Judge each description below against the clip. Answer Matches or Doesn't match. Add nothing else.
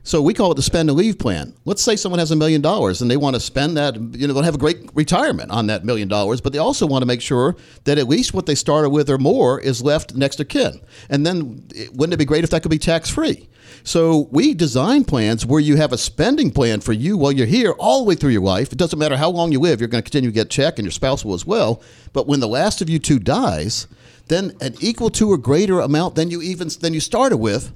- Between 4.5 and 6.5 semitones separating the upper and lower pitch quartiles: Matches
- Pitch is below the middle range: Doesn't match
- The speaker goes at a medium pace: Doesn't match